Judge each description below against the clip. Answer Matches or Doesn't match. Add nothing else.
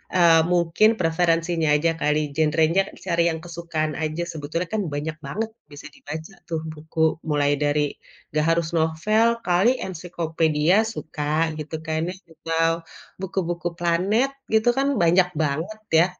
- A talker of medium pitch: Matches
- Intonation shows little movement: Matches